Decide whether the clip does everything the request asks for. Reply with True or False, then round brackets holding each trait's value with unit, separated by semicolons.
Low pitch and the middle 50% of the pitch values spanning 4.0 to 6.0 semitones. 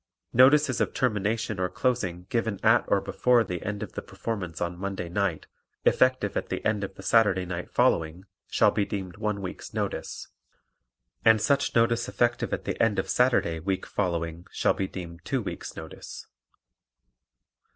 True (100 Hz; 4.3 semitones)